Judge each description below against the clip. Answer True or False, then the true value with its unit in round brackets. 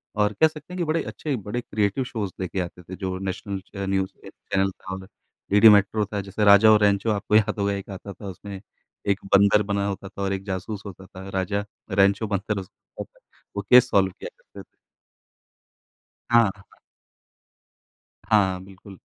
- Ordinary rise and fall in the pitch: False (1.6 semitones)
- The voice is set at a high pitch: False (100 Hz)